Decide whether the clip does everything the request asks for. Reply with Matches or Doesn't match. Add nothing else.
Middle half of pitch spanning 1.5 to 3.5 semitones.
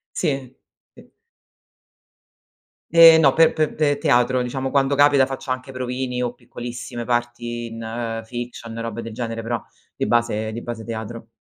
Matches